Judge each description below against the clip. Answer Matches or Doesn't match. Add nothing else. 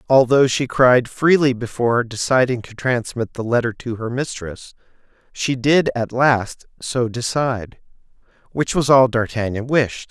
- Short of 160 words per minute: Matches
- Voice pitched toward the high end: Doesn't match